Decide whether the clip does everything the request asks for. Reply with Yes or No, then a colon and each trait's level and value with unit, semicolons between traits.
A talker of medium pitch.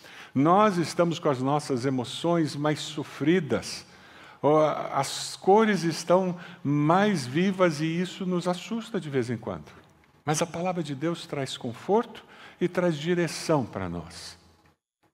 Yes: medium, 165 Hz